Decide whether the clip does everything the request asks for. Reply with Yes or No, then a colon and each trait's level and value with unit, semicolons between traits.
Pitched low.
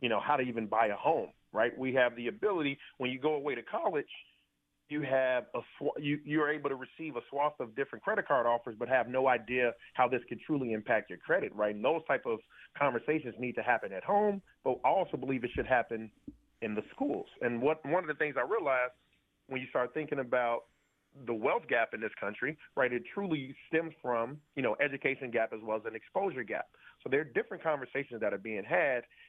Yes: low, 130 Hz